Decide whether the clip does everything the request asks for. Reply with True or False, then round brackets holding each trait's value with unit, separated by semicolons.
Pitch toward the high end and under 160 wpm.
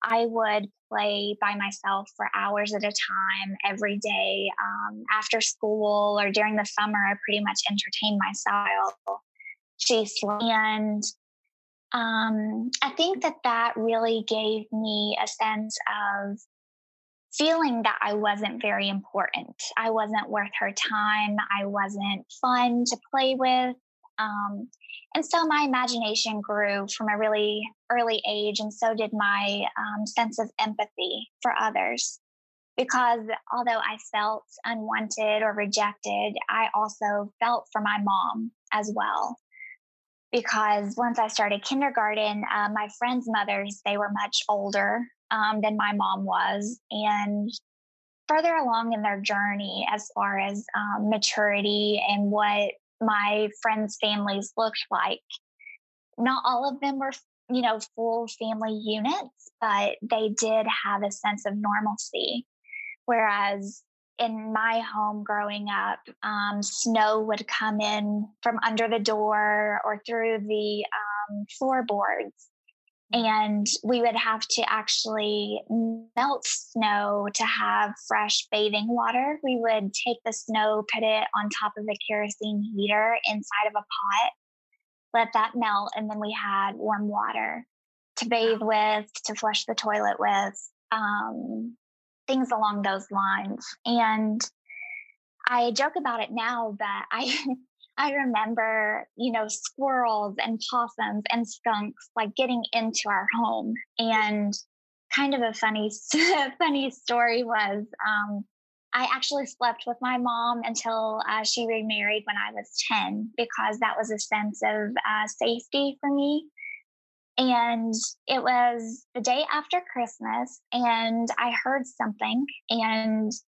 True (220 Hz; 135 wpm)